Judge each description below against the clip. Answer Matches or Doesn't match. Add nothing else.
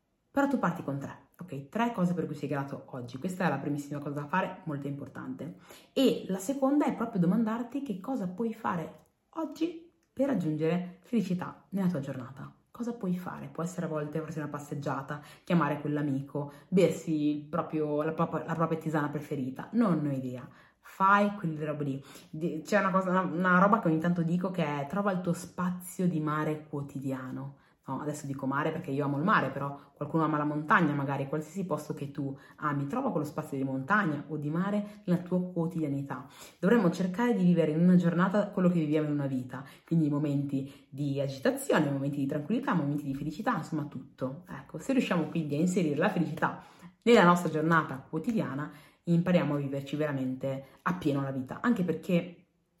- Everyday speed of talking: Doesn't match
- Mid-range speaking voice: Matches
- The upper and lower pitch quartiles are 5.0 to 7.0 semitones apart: Doesn't match